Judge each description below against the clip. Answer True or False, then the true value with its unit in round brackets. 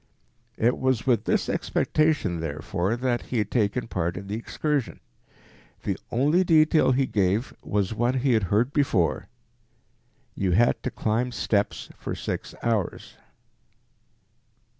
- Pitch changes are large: False (4.8 semitones)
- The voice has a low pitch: True (115 Hz)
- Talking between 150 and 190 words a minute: False (135 wpm)